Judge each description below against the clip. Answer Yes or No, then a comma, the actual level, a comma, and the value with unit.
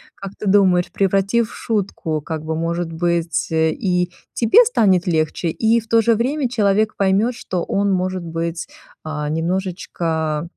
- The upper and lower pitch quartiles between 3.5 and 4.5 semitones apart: Yes, average, 4.0 semitones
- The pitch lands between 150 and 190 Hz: Yes, medium, 185 Hz